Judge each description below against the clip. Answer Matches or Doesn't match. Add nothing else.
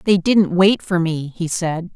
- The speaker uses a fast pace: Matches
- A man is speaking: Doesn't match